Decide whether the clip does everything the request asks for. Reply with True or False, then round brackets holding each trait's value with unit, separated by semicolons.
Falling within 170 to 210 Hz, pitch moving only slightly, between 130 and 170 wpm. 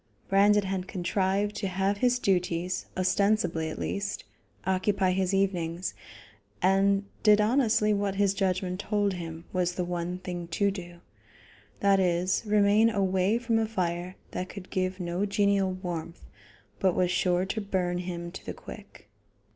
True (190 Hz; 2.1 semitones; 150 wpm)